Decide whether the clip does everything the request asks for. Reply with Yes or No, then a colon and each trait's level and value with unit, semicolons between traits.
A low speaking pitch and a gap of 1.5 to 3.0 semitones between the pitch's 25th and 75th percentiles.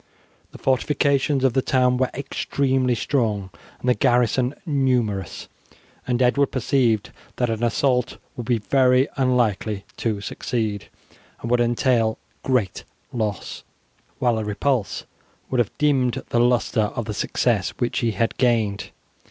Yes: low, 125 Hz; average, 2.7 semitones